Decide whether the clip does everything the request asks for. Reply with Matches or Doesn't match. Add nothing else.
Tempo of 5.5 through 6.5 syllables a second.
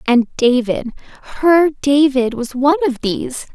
Doesn't match